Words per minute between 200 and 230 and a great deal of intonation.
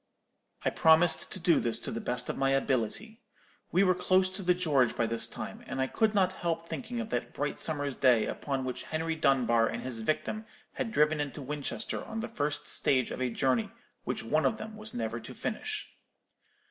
Yes: fast, 205 wpm; wide, 6.5 semitones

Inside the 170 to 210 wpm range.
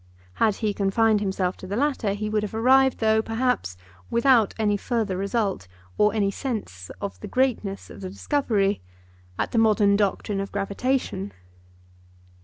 No: average, 155 wpm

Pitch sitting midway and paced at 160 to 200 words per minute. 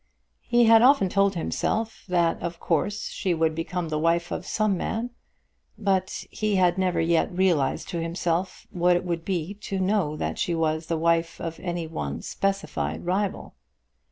Yes: medium, 175 Hz; average, 170 wpm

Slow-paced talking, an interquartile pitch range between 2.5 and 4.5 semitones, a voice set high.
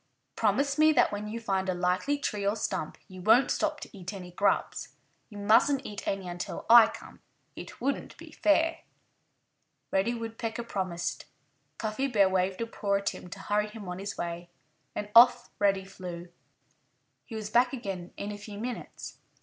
No: average, 175 wpm; average, 3.5 semitones; high, 205 Hz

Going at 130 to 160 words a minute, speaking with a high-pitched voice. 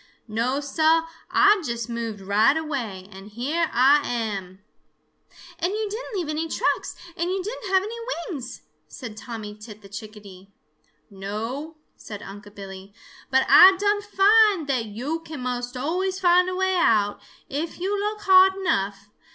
Yes: average, 155 wpm; very high, 275 Hz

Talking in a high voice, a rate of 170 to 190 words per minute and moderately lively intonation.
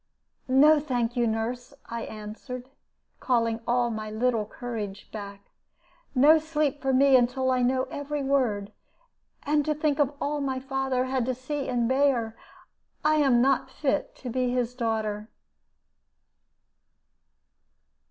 No: very high, 255 Hz; slow, 135 wpm; average, 3.2 semitones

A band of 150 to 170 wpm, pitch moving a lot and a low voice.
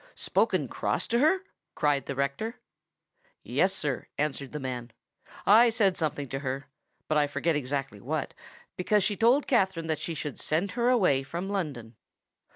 No: average, 155 wpm; wide, 6.5 semitones; medium, 155 Hz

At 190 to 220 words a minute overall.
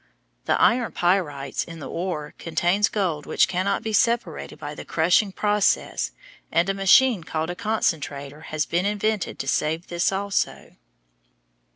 No: average, 150 wpm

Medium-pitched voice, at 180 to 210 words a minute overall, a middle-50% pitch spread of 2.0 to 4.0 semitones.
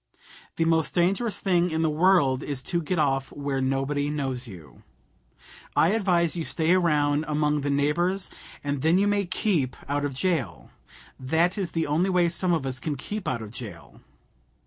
No: medium, 155 Hz; average, 185 wpm; average, 4.4 semitones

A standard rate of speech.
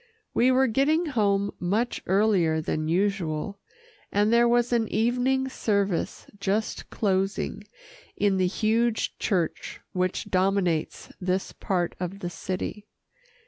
No: slow, 120 wpm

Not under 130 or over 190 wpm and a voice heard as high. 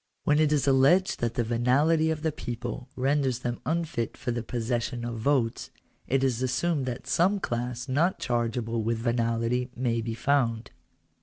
No: average, 170 wpm; low, 125 Hz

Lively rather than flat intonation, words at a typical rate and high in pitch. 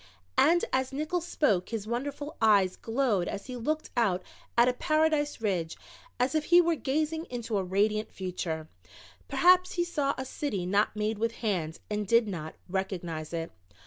Yes: wide, 7.4 semitones; average, 165 wpm; high, 230 Hz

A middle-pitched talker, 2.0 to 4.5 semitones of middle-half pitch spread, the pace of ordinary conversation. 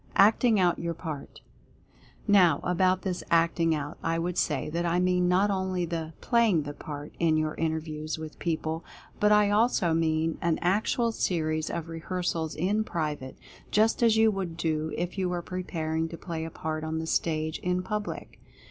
Yes: medium, 170 Hz; average, 2.8 semitones; average, 180 wpm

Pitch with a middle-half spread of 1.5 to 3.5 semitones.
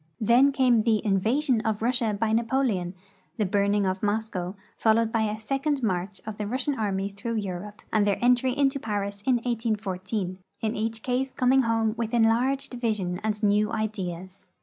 Yes: average, 3.1 semitones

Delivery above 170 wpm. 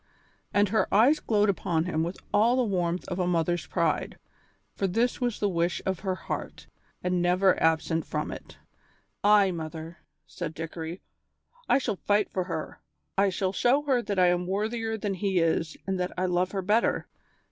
Yes: average, 180 wpm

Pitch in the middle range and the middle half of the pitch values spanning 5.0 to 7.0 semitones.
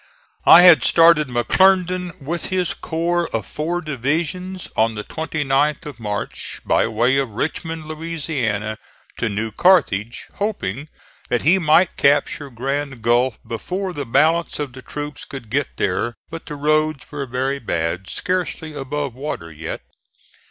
Yes: medium, 145 Hz; wide, 5.6 semitones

